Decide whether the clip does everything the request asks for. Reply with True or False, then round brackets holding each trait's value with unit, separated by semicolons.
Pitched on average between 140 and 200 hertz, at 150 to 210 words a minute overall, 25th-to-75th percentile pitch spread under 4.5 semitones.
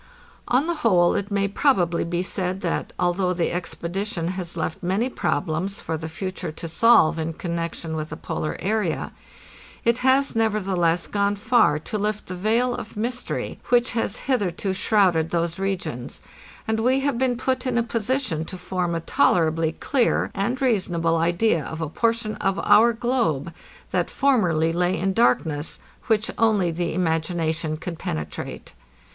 False (185 Hz; 160 wpm; 5.3 semitones)